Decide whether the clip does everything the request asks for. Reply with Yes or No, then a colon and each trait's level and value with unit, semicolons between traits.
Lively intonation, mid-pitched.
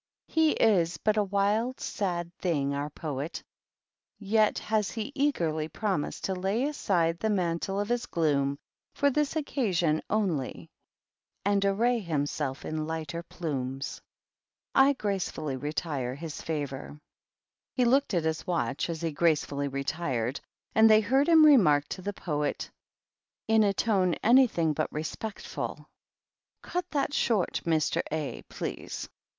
Yes: wide, 6.3 semitones; medium, 175 Hz